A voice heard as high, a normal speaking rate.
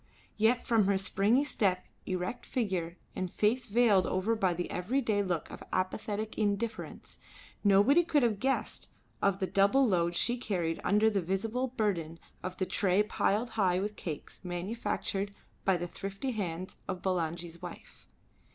Yes: high, 200 Hz; average, 155 wpm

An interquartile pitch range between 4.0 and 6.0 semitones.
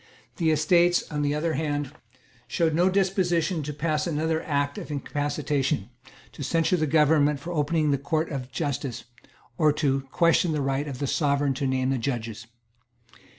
No: narrow, 2.6 semitones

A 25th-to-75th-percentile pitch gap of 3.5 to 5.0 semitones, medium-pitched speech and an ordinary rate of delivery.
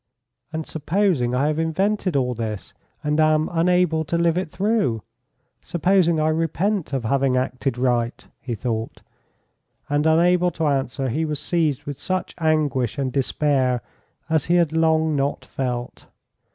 Yes: average, 4.2 semitones; medium, 155 Hz; average, 150 wpm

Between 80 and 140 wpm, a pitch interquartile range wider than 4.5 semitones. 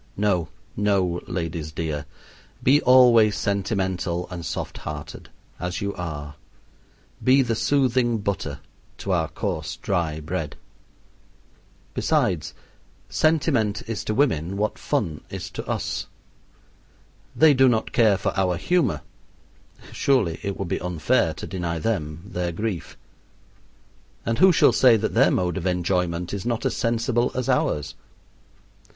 Yes: slow, 135 wpm; average, 5.3 semitones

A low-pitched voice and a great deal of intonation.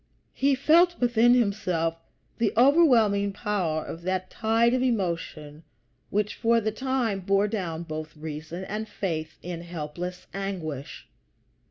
No: high, 195 Hz; wide, 5.7 semitones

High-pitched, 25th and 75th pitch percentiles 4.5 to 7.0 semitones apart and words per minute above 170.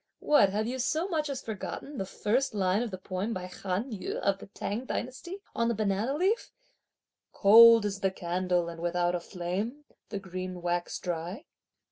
Yes: high, 200 Hz; average, 4.9 semitones; average, 180 wpm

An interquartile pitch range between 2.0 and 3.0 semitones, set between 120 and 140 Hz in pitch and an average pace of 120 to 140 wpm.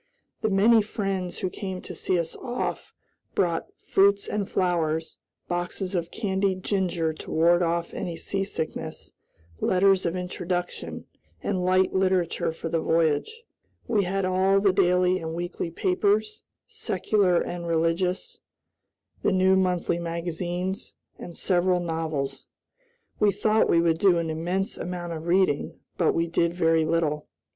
No: narrow, 2.4 semitones; medium, 180 Hz; slow, 135 wpm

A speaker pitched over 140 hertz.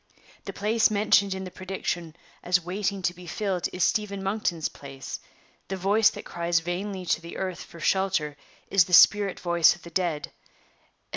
Yes: medium, 185 Hz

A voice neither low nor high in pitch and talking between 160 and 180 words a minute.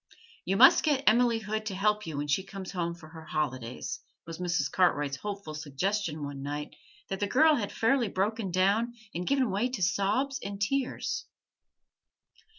No: high, 195 Hz; average, 170 wpm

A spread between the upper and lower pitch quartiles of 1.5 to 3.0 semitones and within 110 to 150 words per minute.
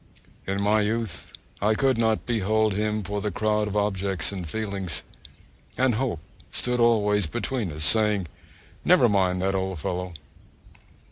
Yes: narrow, 2.4 semitones; average, 145 wpm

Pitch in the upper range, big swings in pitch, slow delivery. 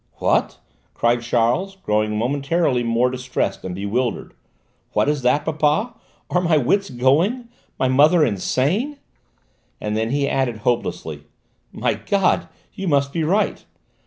No: medium, 140 Hz; wide, 6.0 semitones; slow, 130 wpm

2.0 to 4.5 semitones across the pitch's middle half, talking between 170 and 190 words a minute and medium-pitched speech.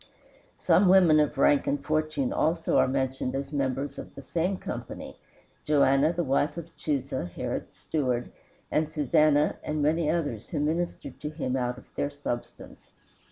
No: narrow, 2.5 semitones; average, 155 wpm; medium, 145 Hz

